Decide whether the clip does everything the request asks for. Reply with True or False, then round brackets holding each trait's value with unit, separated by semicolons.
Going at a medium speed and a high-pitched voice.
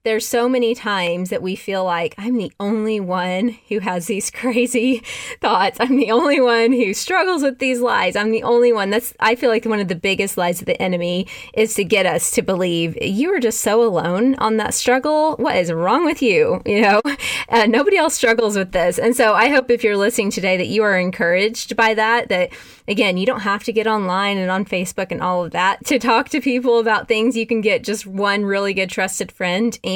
False (230 wpm; 220 Hz)